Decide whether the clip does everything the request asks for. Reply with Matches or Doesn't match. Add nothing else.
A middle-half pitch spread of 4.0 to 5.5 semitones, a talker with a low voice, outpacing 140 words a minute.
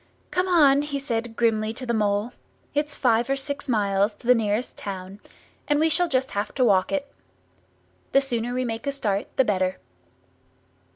Doesn't match